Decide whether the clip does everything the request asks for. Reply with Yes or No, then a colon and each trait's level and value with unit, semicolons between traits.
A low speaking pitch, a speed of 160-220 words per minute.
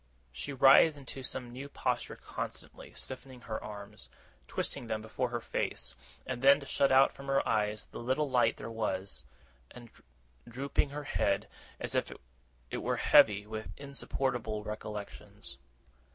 No: low, 120 Hz; average, 150 wpm